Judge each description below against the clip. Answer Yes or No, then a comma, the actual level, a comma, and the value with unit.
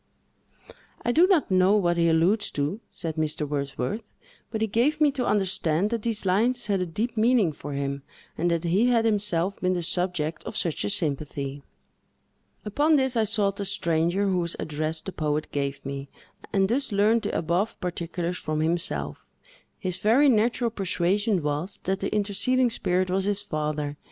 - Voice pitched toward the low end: No, medium, 185 Hz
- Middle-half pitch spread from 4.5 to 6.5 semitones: Yes, average, 5.2 semitones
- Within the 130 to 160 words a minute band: No, average, 175 wpm